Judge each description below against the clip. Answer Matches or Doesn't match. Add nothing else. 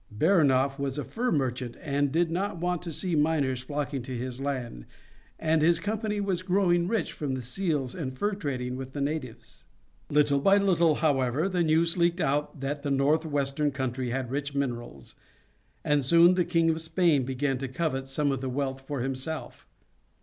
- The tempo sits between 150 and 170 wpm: Doesn't match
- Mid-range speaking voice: Matches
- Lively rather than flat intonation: Doesn't match